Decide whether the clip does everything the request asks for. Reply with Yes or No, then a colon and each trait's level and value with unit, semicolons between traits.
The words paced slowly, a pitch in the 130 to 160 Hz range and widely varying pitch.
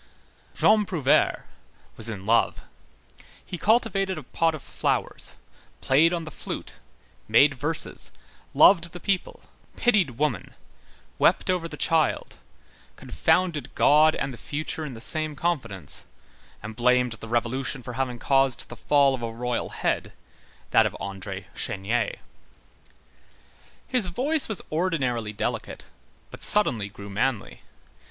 Yes: slow, 130 wpm; low, 135 Hz; wide, 6.2 semitones